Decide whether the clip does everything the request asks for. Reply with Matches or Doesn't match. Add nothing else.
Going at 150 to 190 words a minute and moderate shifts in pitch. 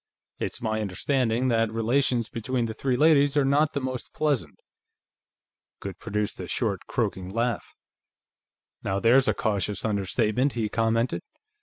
Doesn't match